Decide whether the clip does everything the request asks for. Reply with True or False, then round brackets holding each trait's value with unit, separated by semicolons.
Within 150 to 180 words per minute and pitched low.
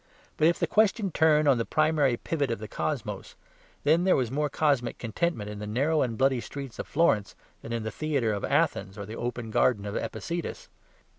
False (205 wpm; 130 Hz)